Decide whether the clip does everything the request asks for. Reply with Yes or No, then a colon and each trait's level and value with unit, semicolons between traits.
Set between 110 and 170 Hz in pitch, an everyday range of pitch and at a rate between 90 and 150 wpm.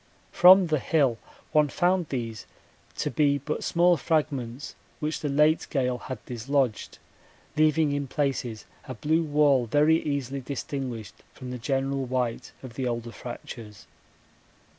Yes: medium, 140 Hz; average, 3.6 semitones; average, 140 wpm